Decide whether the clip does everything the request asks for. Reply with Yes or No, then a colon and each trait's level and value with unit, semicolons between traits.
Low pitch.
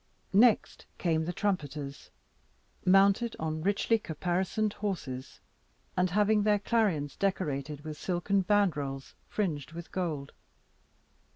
No: medium, 180 Hz